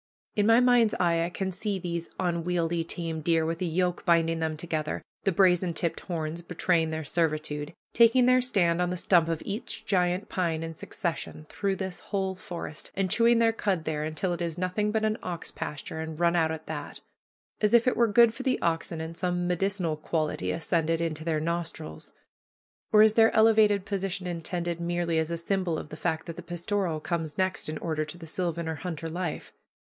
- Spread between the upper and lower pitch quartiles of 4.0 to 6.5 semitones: No, average, 3.0 semitones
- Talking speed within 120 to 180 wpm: No, average, 200 wpm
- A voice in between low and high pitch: Yes, medium, 175 Hz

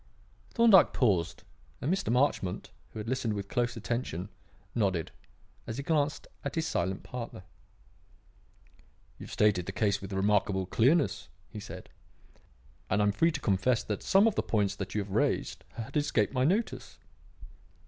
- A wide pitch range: Yes, wide, 5.9 semitones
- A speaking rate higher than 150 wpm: Yes, average, 160 wpm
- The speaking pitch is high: No, low, 115 Hz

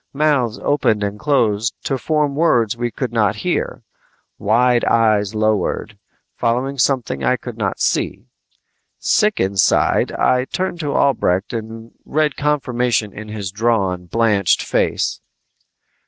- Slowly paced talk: Yes, slow, 125 wpm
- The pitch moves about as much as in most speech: Yes, average, 4.6 semitones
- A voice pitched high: No, low, 115 Hz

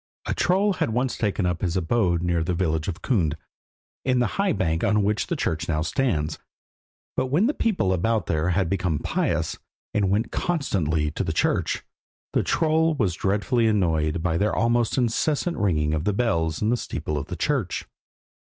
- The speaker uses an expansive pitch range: Yes, wide, 6.8 semitones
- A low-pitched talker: Yes, low, 100 Hz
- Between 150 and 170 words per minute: No, average, 180 wpm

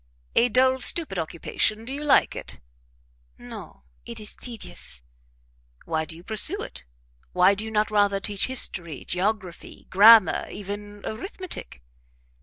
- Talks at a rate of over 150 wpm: No, slow, 135 wpm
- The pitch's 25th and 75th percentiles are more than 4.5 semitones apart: No, average, 4.1 semitones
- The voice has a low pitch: No, high, 210 Hz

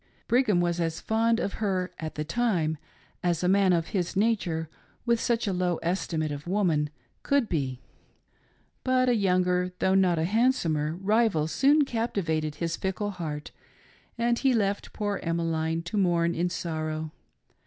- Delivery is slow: No, average, 155 wpm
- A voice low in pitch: No, medium, 180 Hz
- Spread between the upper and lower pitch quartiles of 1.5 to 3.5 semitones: No, average, 4.7 semitones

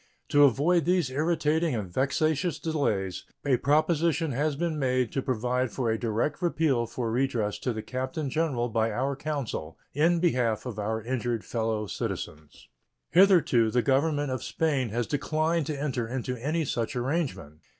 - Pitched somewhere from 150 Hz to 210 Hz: No, low, 130 Hz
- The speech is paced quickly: No, average, 160 wpm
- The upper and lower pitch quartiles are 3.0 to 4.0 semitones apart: No, average, 4.9 semitones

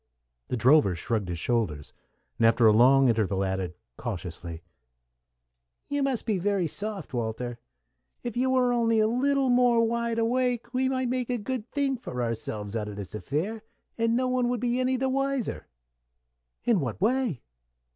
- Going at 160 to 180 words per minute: Yes, average, 165 wpm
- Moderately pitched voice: No, high, 215 Hz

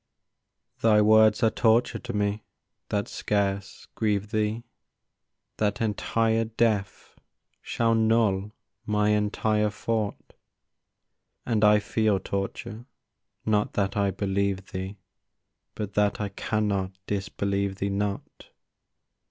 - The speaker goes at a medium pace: No, slow, 105 wpm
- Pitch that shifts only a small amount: Yes, narrow, 1.6 semitones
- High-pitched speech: No, low, 105 Hz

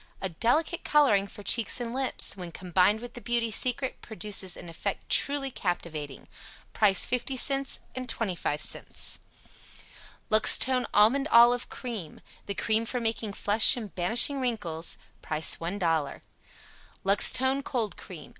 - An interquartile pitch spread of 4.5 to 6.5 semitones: Yes, average, 5.3 semitones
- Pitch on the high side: Yes, high, 220 Hz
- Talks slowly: Yes, slow, 120 wpm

